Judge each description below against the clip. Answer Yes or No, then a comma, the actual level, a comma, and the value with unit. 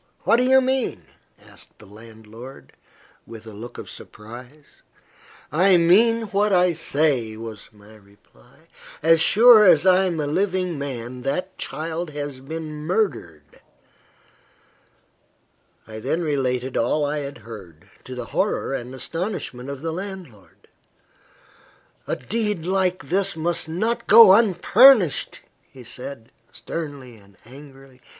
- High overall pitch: No, medium, 150 Hz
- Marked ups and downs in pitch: Yes, wide, 7.2 semitones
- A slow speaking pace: Yes, slow, 130 wpm